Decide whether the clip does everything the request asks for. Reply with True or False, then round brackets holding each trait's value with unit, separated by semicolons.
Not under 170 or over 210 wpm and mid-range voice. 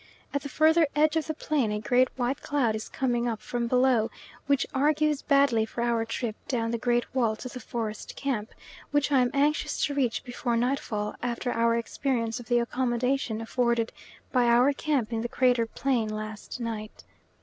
False (185 wpm; 245 Hz)